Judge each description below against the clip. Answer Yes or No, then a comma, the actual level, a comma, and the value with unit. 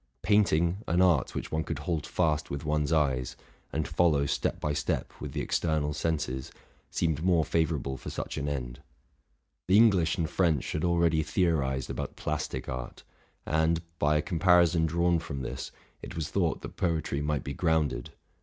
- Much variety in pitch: No, average, 2.7 semitones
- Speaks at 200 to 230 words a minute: No, average, 175 wpm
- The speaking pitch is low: Yes, very low, 80 Hz